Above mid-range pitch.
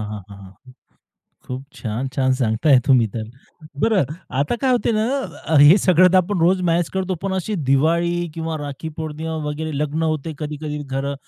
No: medium, 155 Hz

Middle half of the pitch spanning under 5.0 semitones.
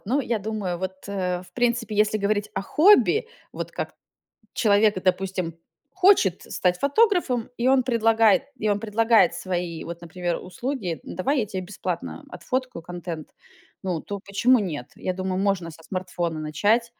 Yes: average, 4.5 semitones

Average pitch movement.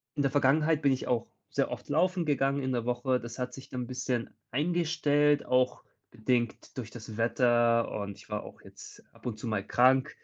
Yes: average, 3.3 semitones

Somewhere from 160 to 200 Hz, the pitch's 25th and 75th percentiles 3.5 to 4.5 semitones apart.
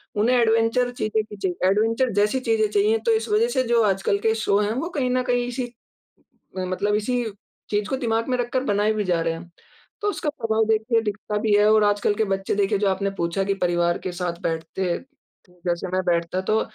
No: high, 215 Hz; average, 4.0 semitones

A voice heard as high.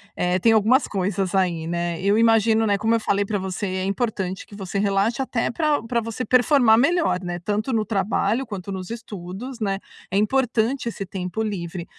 Yes: high, 205 Hz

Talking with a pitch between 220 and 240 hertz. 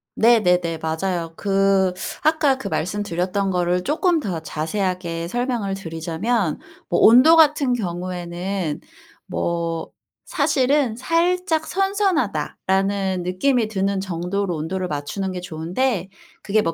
No: high, 195 Hz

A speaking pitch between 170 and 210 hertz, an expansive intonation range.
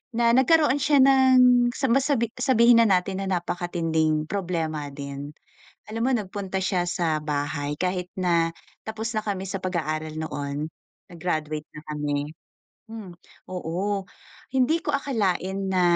Yes: medium, 185 Hz; wide, 6.6 semitones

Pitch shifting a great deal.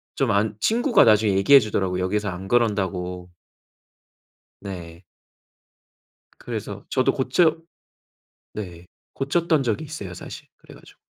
Yes: wide, 6.7 semitones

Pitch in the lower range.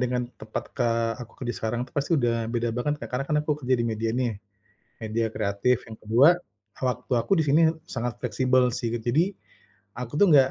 Yes: low, 125 Hz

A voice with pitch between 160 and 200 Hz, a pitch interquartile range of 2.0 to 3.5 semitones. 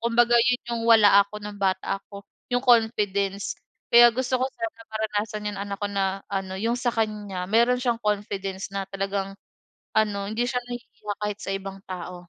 No: high, 210 Hz; average, 2.9 semitones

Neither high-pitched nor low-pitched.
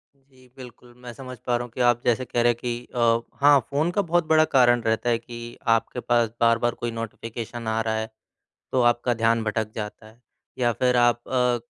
No: low, 120 Hz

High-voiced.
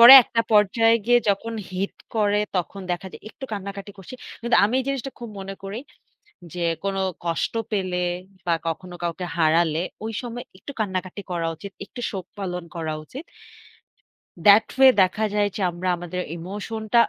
Yes: high, 195 Hz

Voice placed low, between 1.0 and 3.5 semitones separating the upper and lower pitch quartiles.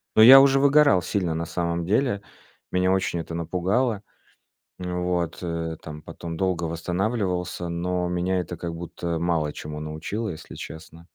Yes: very low, 90 Hz; narrow, 2.4 semitones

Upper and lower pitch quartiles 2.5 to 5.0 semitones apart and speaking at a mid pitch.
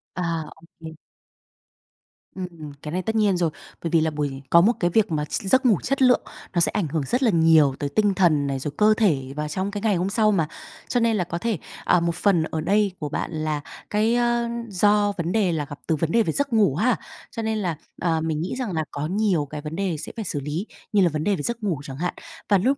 No: wide, 5.4 semitones; medium, 180 Hz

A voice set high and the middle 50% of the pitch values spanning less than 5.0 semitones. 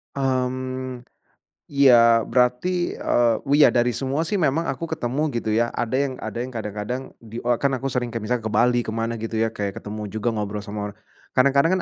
No: low, 120 Hz; average, 3.0 semitones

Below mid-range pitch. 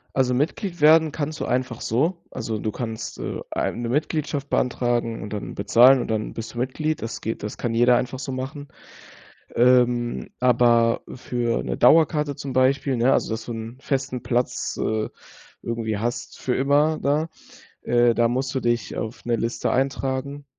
Yes: low, 125 Hz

